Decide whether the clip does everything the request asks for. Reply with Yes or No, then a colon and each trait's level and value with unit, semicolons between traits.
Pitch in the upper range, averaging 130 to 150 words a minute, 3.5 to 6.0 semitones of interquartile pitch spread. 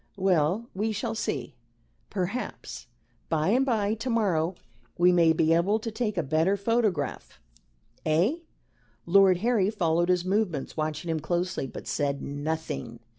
No: medium, 180 Hz; average, 140 wpm; average, 4.9 semitones